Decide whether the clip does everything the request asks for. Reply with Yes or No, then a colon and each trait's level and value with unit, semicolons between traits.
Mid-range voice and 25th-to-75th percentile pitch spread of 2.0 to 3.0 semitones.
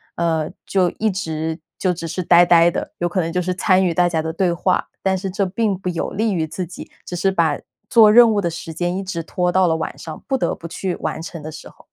Yes: medium, 175 Hz; narrow, 2.4 semitones